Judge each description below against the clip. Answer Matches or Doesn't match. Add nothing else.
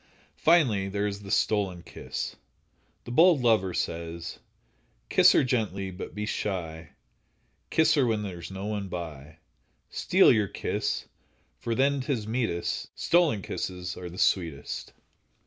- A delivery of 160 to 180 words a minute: Doesn't match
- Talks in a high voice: Doesn't match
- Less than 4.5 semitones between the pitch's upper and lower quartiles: Doesn't match